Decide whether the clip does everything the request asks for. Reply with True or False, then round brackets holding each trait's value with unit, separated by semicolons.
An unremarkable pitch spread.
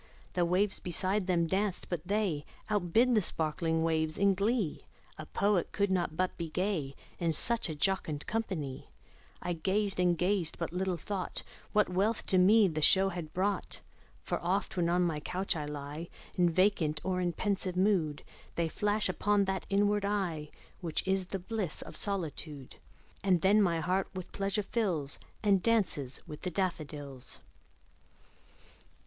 True (3.6 semitones)